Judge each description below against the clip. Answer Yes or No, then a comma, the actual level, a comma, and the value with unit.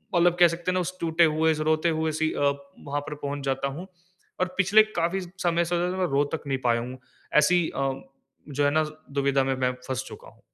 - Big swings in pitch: No, average, 4.0 semitones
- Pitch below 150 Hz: No, medium, 160 Hz